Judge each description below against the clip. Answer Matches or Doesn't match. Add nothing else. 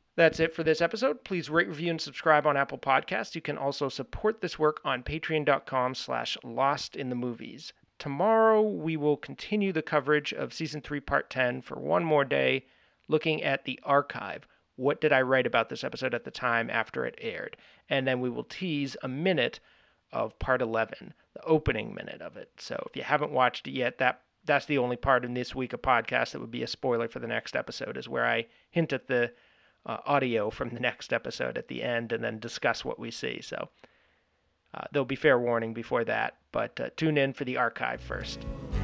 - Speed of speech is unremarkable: Doesn't match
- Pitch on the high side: Doesn't match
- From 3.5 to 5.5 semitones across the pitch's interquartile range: Matches